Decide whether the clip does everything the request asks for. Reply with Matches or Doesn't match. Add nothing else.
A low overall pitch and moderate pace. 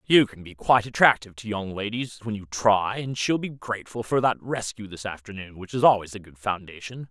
Doesn't match